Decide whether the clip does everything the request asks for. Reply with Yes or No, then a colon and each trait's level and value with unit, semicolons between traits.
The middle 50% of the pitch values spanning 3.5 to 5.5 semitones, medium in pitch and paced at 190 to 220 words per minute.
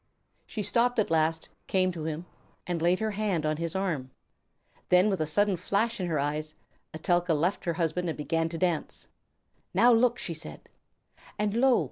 Yes: average, 4.2 semitones; medium, 175 Hz; average, 195 wpm